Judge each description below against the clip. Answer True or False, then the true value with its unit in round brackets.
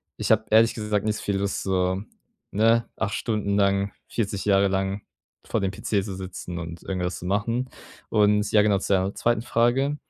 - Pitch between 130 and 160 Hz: False (100 Hz)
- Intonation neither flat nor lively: False (2.2 semitones)